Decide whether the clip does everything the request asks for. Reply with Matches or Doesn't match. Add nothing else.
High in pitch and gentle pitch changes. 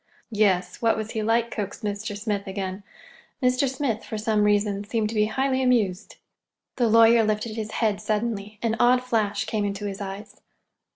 Matches